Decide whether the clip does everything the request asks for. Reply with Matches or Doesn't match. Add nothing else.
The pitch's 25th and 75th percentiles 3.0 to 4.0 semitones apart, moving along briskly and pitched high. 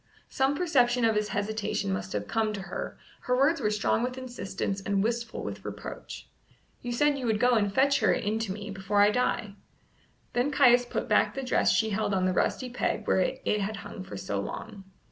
Matches